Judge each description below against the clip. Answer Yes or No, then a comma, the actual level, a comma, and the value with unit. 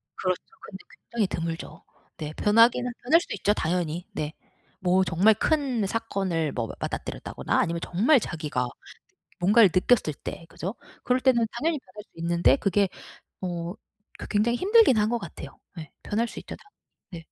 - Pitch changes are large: Yes, wide, 5.8 semitones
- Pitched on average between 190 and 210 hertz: Yes, high, 195 Hz